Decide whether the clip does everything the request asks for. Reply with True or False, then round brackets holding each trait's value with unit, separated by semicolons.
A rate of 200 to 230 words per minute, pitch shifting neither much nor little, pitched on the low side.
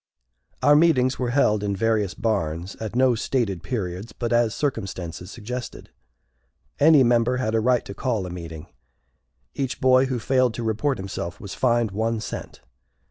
False (160 wpm; 4.4 semitones; 115 Hz)